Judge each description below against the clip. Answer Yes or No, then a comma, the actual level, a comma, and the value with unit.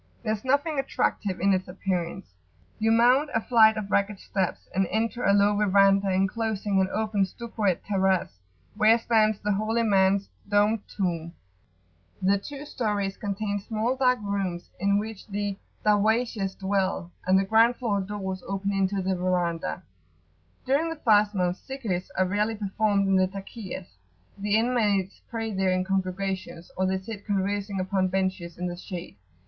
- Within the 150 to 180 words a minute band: Yes, average, 160 wpm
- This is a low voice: No, high, 200 Hz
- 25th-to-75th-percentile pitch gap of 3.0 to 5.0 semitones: No, narrow, 2.5 semitones